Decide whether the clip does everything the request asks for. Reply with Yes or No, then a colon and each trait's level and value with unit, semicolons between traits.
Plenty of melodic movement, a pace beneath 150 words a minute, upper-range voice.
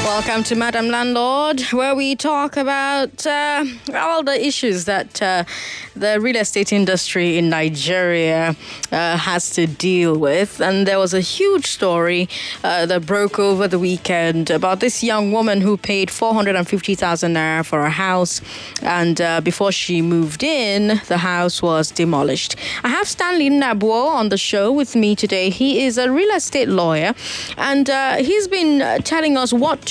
No: wide, 6.9 semitones; average, 165 wpm; high, 200 Hz